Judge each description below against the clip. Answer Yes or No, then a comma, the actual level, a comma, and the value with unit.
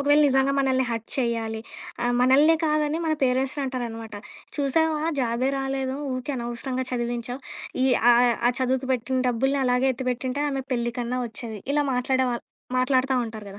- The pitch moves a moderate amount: No, narrow, 2.1 semitones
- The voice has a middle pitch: No, very high, 255 Hz